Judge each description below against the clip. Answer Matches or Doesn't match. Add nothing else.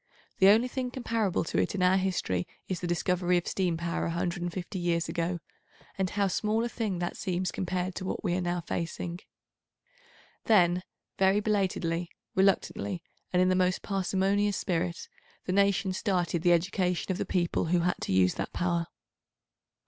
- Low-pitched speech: Doesn't match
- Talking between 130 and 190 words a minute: Matches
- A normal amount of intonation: Doesn't match